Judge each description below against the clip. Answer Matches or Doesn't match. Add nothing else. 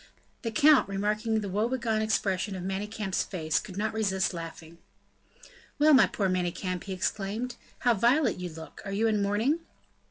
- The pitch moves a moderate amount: Matches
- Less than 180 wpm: Matches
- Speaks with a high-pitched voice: Matches